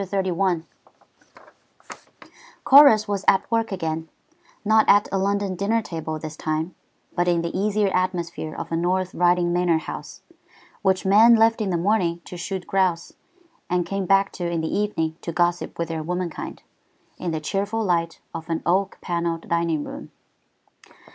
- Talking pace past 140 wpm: Yes, average, 160 wpm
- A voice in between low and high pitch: Yes, medium, 180 Hz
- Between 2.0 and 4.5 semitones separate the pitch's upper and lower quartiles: Yes, average, 2.8 semitones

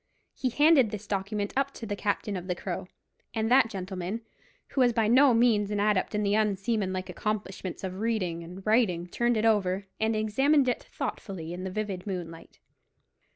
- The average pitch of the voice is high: Yes, high, 210 Hz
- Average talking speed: Yes, average, 180 wpm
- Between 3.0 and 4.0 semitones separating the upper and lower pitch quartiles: Yes, average, 3.3 semitones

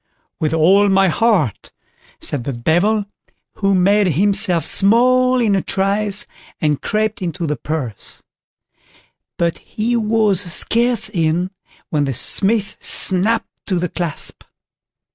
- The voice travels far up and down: No, average, 4.7 semitones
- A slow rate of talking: Yes, slow, 125 wpm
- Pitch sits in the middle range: No, high, 195 Hz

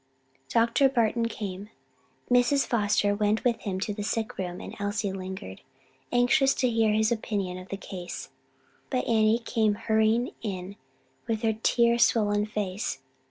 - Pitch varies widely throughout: No, narrow, 2.4 semitones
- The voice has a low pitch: No, high, 215 Hz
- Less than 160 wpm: Yes, average, 150 wpm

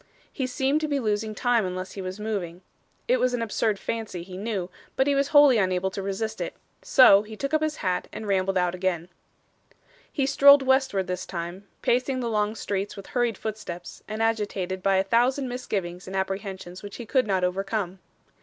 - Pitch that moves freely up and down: No, average, 4.8 semitones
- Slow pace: No, average, 195 wpm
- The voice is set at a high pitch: Yes, high, 205 Hz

